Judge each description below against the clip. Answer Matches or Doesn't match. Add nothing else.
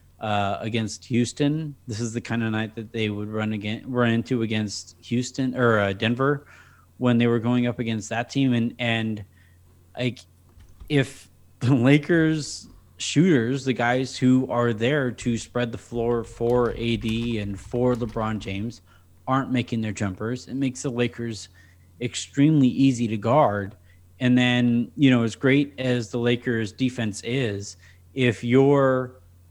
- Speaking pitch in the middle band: Doesn't match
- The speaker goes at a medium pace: Matches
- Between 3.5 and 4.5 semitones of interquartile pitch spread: Doesn't match